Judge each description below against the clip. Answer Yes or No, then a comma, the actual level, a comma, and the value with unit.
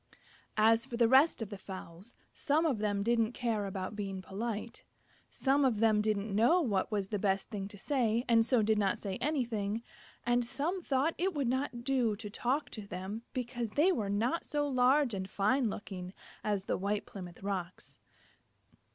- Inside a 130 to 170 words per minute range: No, average, 185 wpm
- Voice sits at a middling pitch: No, high, 225 Hz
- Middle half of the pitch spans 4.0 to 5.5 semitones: Yes, average, 4.3 semitones